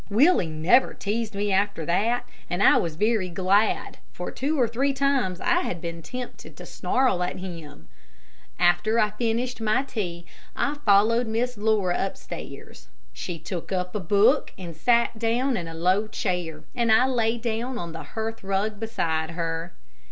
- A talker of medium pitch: No, high, 210 Hz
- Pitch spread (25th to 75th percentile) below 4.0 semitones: No, average, 5.0 semitones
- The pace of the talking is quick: No, average, 165 wpm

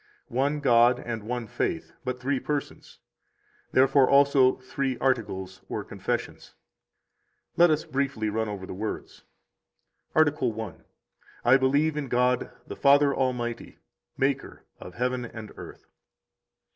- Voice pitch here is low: Yes, low, 125 Hz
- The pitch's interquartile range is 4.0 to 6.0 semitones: No, average, 3.0 semitones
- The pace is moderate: No, slow, 130 wpm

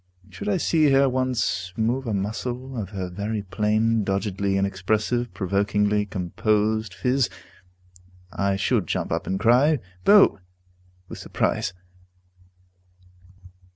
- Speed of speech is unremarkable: No, slow, 115 wpm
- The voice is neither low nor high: No, low, 105 Hz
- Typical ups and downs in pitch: Yes, average, 4.1 semitones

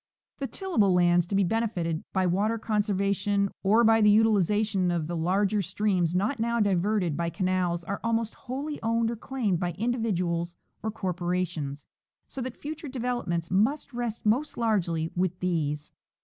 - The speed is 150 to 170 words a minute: Yes, average, 160 wpm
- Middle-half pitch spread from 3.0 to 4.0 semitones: No, average, 4.4 semitones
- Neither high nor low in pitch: No, high, 200 Hz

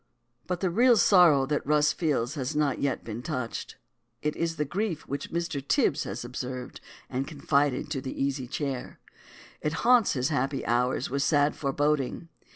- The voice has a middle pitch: Yes, medium, 145 Hz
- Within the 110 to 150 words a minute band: No, average, 165 wpm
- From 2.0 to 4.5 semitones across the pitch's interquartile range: Yes, average, 3.4 semitones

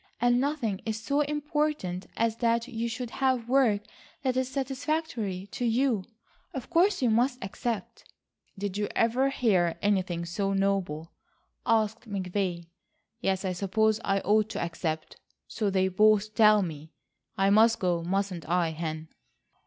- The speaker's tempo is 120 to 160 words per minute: Yes, average, 145 wpm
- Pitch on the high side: Yes, high, 215 Hz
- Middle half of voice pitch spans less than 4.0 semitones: No, average, 4.6 semitones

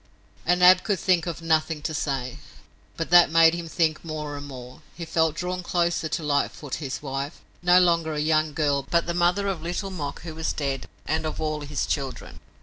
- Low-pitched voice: No, medium, 160 Hz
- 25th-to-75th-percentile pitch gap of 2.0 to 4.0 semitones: Yes, average, 2.8 semitones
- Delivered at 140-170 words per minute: No, fast, 205 wpm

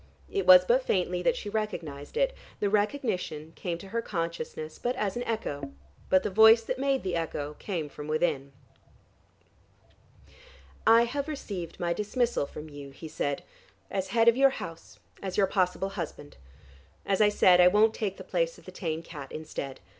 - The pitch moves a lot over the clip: Yes, wide, 5.9 semitones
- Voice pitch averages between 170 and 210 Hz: Yes, high, 190 Hz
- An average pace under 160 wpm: No, average, 175 wpm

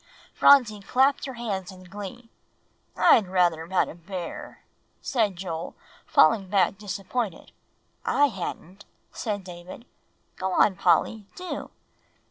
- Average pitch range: Yes, average, 3.7 semitones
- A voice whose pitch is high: Yes, high, 195 Hz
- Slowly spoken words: Yes, slow, 120 wpm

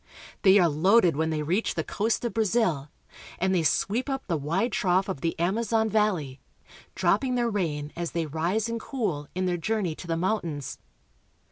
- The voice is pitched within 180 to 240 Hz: Yes, medium, 185 Hz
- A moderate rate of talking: Yes, average, 190 wpm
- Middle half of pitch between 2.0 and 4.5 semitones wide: No, wide, 5.5 semitones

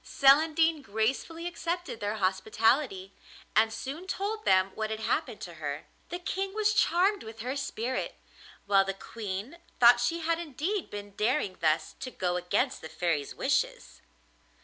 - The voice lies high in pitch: Yes, high, 240 Hz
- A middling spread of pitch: No, wide, 8.9 semitones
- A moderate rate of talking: Yes, average, 150 wpm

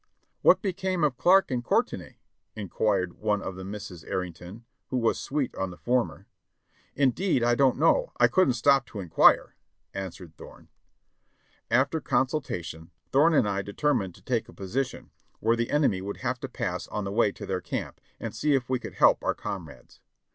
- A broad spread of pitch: Yes, wide, 5.9 semitones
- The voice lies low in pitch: Yes, low, 120 Hz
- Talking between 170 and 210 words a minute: Yes, average, 180 wpm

